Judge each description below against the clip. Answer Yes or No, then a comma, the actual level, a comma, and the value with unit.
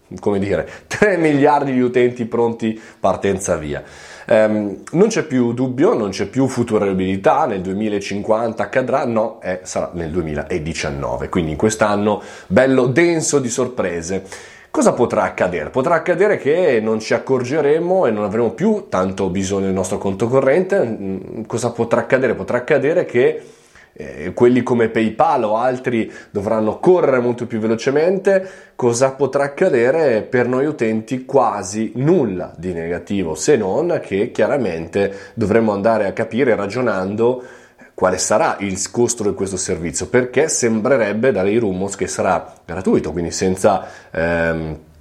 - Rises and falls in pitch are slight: No, average, 4.8 semitones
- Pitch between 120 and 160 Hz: No, low, 110 Hz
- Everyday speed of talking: Yes, average, 140 wpm